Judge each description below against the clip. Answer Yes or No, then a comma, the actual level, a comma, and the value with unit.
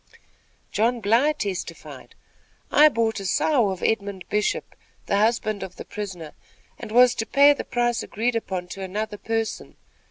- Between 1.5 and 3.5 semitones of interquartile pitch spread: Yes, average, 3.2 semitones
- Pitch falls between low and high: No, high, 220 Hz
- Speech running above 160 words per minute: No, average, 155 wpm